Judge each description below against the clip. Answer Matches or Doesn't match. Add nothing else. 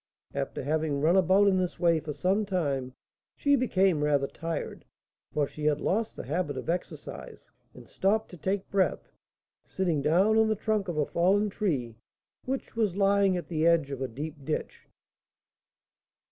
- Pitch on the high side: Doesn't match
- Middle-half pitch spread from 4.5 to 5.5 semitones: Matches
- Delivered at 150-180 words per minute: Matches